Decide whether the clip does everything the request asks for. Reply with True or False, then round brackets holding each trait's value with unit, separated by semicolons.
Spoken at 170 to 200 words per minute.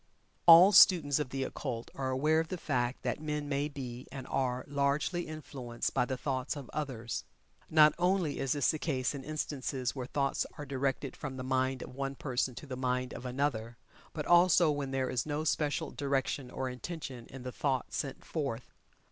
True (190 wpm)